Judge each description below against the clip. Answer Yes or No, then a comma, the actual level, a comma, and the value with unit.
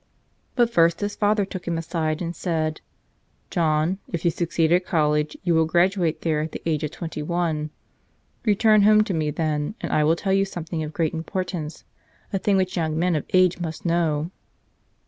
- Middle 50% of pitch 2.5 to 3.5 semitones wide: Yes, average, 2.9 semitones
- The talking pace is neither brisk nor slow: Yes, average, 190 wpm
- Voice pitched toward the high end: No, medium, 170 Hz